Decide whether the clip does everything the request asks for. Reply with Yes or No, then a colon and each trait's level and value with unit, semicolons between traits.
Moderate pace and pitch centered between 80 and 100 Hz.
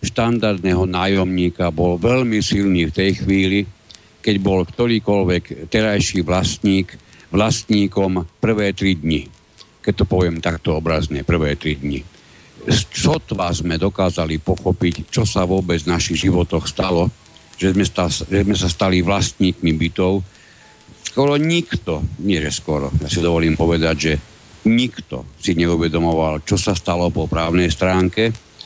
Yes: average, 135 wpm; very low, 90 Hz